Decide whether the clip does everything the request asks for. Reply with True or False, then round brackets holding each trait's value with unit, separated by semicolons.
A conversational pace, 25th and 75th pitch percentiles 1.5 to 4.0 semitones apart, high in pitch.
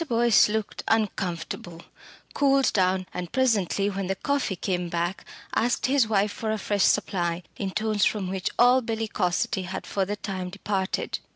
True (160 wpm; 3.3 semitones; 200 Hz)